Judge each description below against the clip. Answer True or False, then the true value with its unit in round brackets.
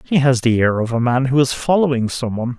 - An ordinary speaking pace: False (280 wpm)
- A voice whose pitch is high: False (125 Hz)